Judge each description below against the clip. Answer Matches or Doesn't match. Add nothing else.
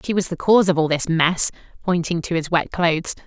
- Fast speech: Matches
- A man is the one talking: Doesn't match